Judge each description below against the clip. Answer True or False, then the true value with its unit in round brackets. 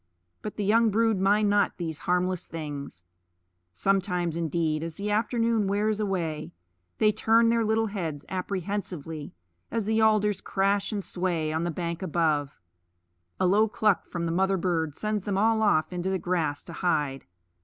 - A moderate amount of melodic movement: True (4.2 semitones)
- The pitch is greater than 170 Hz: True (190 Hz)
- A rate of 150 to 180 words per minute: True (165 wpm)